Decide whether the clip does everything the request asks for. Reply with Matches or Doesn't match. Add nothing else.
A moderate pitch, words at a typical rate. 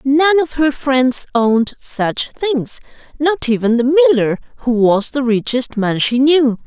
Doesn't match